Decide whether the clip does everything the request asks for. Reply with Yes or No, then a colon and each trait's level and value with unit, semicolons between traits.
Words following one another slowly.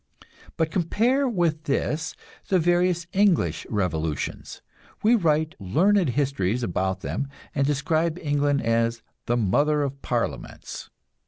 Yes: slow, 115 wpm